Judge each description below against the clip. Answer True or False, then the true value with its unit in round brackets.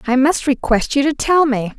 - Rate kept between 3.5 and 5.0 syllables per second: True (4.9 syllables/s)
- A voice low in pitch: False (270 Hz)